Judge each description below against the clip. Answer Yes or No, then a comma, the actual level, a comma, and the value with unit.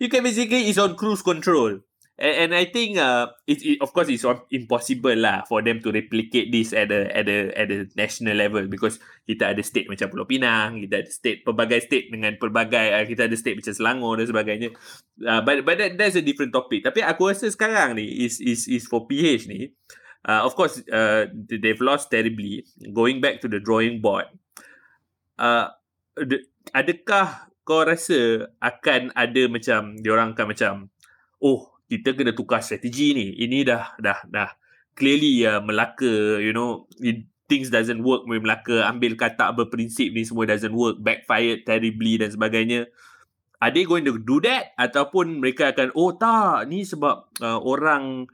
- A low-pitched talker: Yes, low, 120 Hz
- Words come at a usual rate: No, fast, 180 wpm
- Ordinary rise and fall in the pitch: Yes, average, 4.7 semitones